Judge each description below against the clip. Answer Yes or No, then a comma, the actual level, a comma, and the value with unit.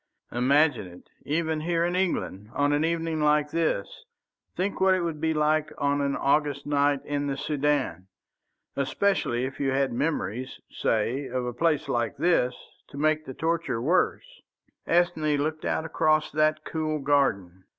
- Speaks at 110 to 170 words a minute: Yes, average, 155 wpm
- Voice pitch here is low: No, medium, 150 Hz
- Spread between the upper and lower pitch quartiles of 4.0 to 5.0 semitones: No, average, 2.9 semitones